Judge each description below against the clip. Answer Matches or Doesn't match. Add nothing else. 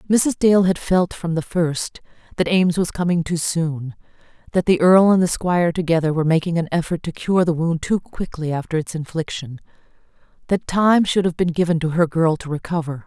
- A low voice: Doesn't match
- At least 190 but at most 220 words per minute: Matches